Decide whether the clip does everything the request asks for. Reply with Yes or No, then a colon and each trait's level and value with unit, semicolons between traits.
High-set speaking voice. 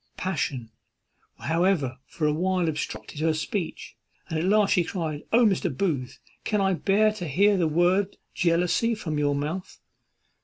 No: medium, 175 Hz